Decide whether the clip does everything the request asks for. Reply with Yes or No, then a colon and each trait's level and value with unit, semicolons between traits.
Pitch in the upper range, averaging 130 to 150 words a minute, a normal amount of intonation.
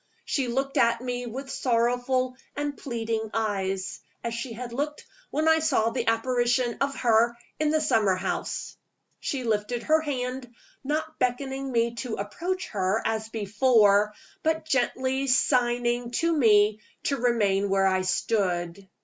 Yes: high, 240 Hz; average, 145 wpm; average, 3.5 semitones